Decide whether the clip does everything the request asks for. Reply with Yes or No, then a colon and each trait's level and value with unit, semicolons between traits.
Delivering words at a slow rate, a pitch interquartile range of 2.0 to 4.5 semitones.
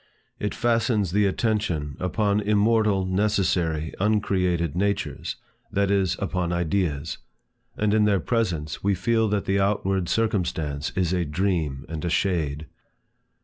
Yes: slow, 130 wpm; average, 3.5 semitones